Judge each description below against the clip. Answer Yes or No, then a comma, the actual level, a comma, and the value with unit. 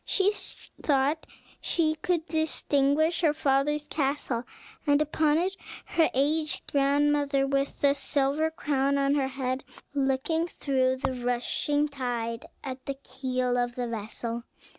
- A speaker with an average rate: No, slow, 130 wpm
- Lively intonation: No, narrow, 2.5 semitones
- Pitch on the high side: Yes, very high, 280 Hz